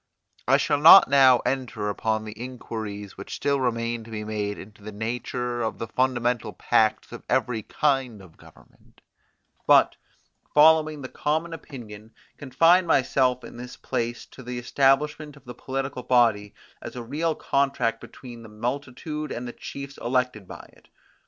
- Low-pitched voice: Yes, low, 125 Hz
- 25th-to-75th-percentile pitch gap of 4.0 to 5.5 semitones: No, average, 3.6 semitones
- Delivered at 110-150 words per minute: No, average, 160 wpm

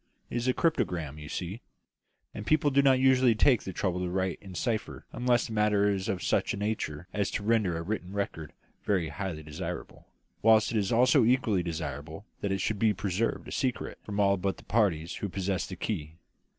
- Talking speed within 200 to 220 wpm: Yes, fast, 205 wpm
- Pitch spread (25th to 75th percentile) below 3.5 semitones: No, average, 4.1 semitones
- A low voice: Yes, low, 100 Hz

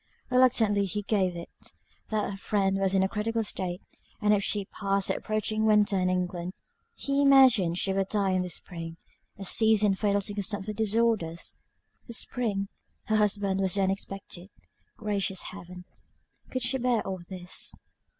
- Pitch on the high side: Yes, high, 200 Hz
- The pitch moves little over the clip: Yes, narrow, 2.3 semitones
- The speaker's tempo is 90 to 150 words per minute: No, average, 160 wpm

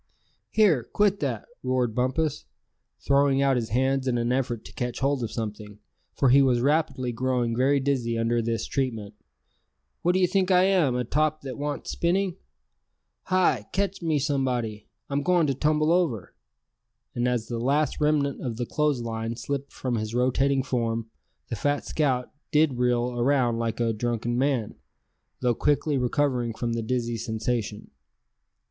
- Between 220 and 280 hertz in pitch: No, low, 130 Hz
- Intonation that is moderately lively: Yes, average, 3.5 semitones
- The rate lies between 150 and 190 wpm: Yes, average, 160 wpm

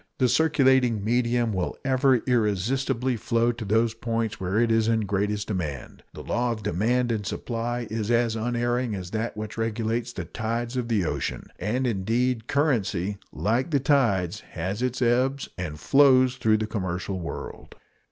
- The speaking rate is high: No, average, 160 wpm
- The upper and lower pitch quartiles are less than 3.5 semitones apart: Yes, average, 2.9 semitones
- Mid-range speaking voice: No, low, 115 Hz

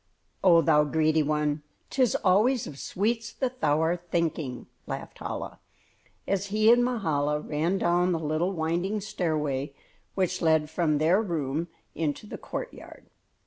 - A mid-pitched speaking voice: Yes, medium, 170 Hz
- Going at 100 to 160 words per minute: Yes, average, 145 wpm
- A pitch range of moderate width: Yes, average, 4.4 semitones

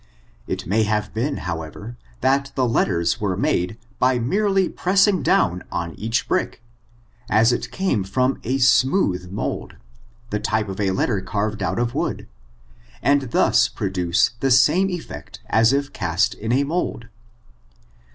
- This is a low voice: Yes, low, 115 Hz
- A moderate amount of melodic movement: No, wide, 5.9 semitones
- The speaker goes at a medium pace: Yes, average, 150 wpm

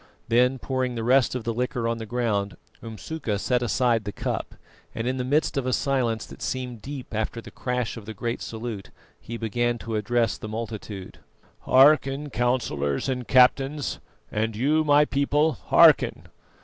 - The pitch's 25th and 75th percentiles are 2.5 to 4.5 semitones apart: Yes, average, 2.8 semitones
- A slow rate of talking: No, average, 170 wpm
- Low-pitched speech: Yes, low, 120 Hz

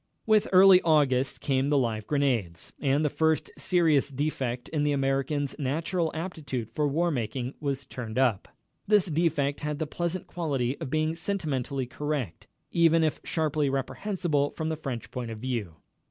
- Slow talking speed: No, average, 160 wpm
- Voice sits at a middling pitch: Yes, medium, 145 Hz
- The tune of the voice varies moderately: Yes, average, 3.6 semitones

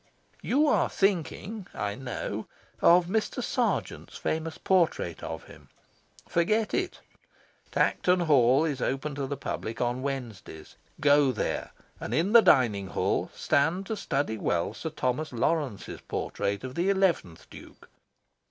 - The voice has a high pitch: No, medium, 145 Hz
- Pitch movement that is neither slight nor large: No, wide, 6.5 semitones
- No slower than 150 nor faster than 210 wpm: No, slow, 135 wpm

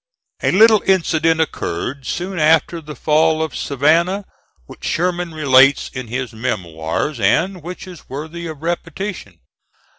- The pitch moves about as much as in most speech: Yes, average, 4.5 semitones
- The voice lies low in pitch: No, medium, 160 Hz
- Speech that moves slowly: Yes, slow, 130 wpm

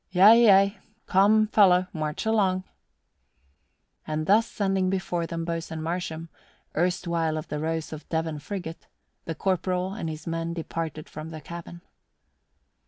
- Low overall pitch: No, medium, 170 Hz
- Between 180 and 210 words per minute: No, slow, 135 wpm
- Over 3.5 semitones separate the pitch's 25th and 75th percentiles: No, average, 3.0 semitones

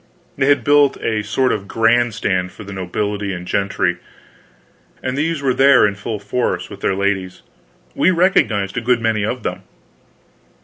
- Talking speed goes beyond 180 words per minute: No, average, 170 wpm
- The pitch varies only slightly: No, average, 4.6 semitones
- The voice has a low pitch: Yes, low, 110 Hz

